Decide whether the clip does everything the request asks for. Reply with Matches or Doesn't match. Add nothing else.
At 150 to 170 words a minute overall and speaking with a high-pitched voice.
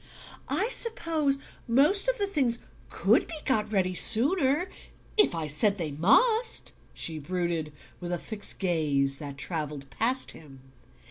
Doesn't match